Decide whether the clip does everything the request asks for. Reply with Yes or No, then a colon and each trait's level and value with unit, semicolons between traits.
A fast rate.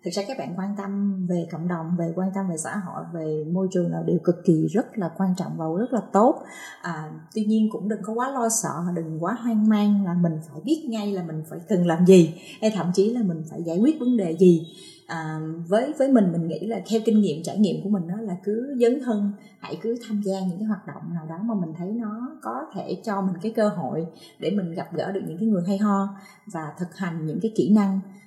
Yes: fast, 260 wpm